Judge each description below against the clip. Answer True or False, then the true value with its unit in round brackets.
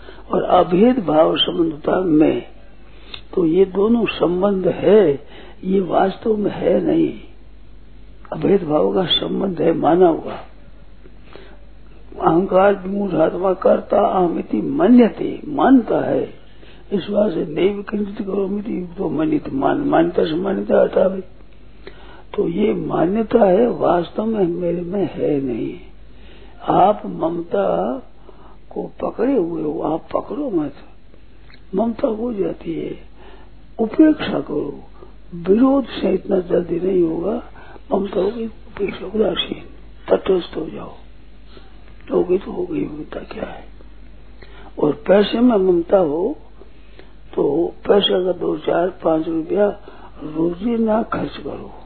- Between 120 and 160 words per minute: False (110 wpm)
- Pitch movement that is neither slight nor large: False (8.3 semitones)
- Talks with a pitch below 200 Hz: False (205 Hz)